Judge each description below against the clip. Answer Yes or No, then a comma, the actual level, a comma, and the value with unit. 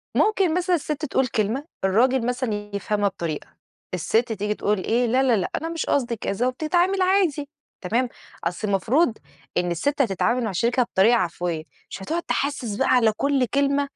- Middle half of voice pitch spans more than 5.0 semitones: Yes, wide, 5.5 semitones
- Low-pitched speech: No, high, 245 Hz